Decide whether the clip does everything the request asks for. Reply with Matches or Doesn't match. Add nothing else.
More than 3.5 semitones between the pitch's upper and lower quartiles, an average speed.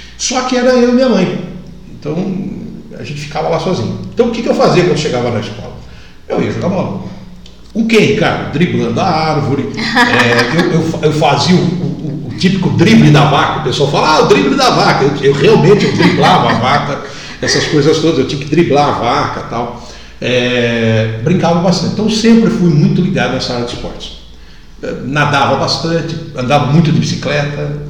Doesn't match